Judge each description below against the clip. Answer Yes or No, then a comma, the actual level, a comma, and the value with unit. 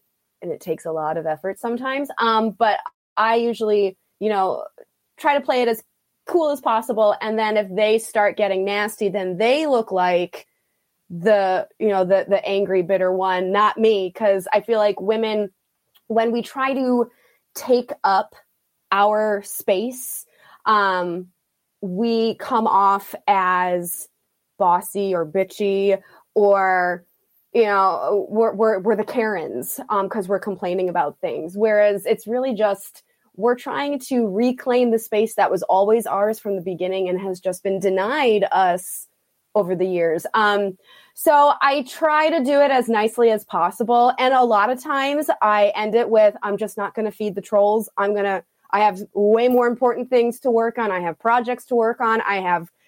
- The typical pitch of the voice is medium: No, high, 210 Hz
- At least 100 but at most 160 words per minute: No, average, 170 wpm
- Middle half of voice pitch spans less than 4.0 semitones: Yes, average, 3.3 semitones